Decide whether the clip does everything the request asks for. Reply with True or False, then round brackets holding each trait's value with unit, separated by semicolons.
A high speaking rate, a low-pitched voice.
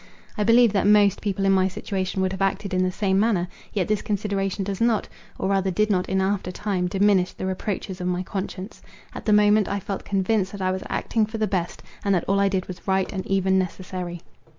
False (230 wpm; 195 Hz)